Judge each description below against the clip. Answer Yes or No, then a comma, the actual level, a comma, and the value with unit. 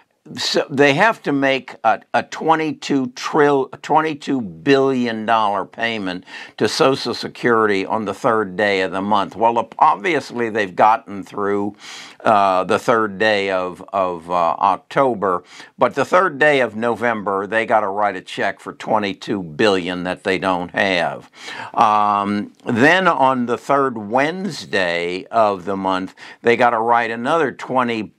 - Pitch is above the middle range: No, low, 115 Hz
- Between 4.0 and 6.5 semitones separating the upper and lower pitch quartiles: Yes, average, 5.3 semitones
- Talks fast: No, average, 145 wpm